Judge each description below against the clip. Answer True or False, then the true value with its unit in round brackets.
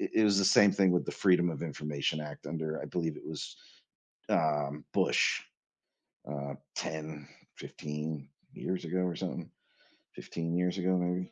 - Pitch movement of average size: True (3.2 semitones)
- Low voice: True (80 Hz)